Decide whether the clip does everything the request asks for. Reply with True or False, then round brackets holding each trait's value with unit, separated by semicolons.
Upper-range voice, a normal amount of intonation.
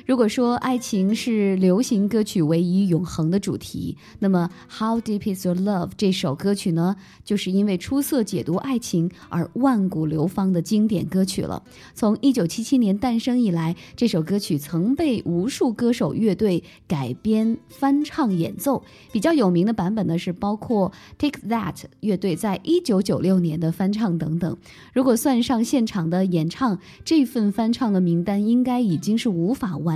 True (200 Hz; 4.9 semitones)